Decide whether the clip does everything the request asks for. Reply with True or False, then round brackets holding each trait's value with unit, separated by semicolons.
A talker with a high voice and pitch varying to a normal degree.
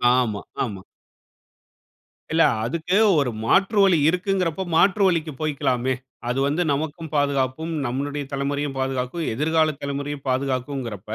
False (145 Hz; 3.7 semitones)